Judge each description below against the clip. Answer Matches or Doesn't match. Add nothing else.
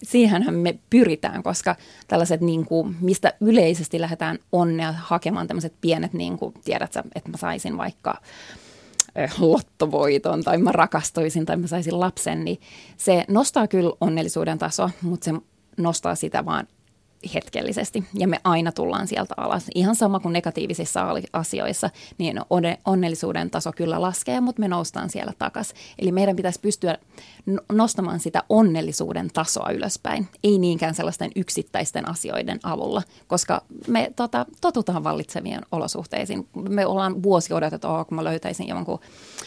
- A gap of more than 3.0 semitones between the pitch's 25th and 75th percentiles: Matches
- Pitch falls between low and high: Matches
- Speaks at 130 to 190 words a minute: Matches